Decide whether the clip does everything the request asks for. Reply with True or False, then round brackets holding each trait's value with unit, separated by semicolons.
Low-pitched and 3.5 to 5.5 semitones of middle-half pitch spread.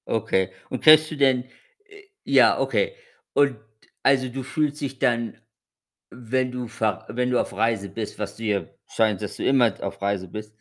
True (120 Hz; 3.9 semitones)